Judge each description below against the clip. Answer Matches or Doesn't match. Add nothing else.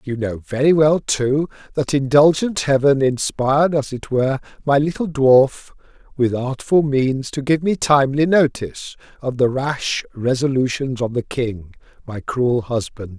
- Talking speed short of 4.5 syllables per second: Matches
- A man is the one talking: Matches